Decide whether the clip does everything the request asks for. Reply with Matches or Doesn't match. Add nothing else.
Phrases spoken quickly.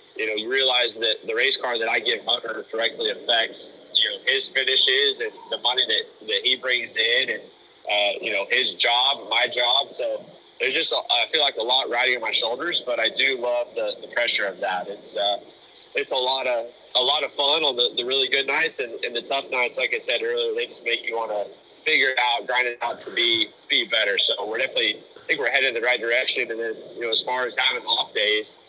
Matches